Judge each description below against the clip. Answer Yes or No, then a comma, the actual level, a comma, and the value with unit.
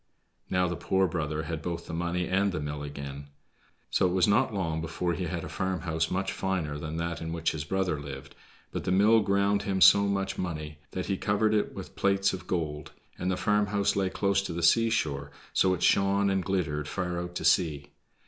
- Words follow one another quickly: Yes, fast, 210 wpm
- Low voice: Yes, very low, 90 Hz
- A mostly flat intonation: No, average, 3.5 semitones